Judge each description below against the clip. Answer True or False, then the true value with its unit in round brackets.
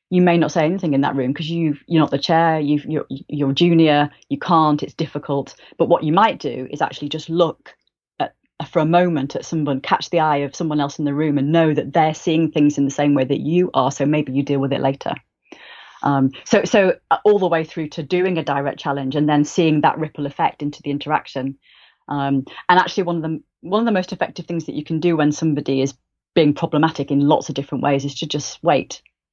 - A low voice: False (155 Hz)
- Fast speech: True (235 wpm)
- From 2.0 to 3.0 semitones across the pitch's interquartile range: True (2.7 semitones)